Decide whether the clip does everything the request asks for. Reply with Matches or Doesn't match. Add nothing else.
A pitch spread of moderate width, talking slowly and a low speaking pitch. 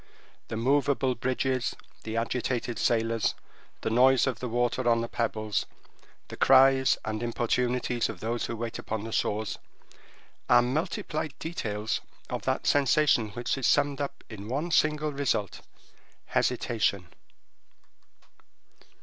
Matches